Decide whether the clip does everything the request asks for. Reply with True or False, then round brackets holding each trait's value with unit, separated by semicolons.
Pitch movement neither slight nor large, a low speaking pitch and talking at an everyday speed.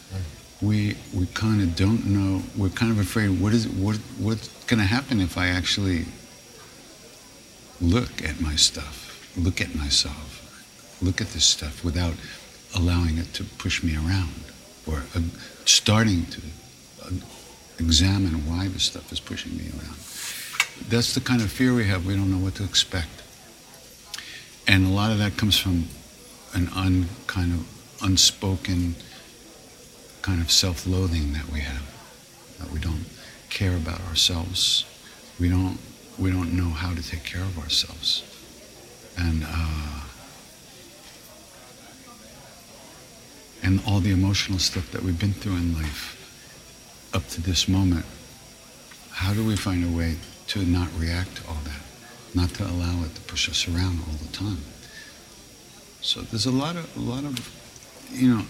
True (3.6 semitones; 90 Hz; 150 wpm)